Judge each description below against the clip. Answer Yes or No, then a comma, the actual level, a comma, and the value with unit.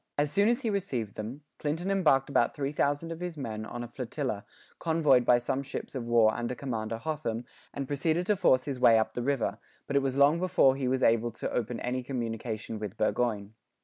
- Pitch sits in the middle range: No, low, 130 Hz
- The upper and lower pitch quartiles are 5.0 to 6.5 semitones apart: No, average, 4.2 semitones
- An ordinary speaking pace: No, fast, 210 wpm